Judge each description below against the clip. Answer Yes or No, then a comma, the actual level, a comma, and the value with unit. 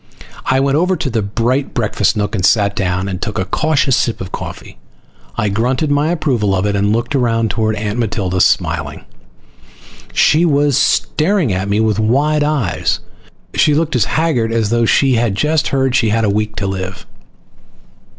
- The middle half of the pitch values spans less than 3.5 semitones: No, wide, 5.4 semitones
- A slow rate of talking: No, average, 180 wpm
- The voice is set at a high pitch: No, low, 115 Hz